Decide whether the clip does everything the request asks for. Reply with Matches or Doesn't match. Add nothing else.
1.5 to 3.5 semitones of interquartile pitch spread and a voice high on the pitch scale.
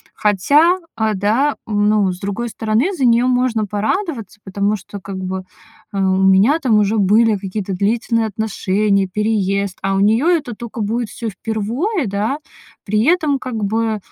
Matches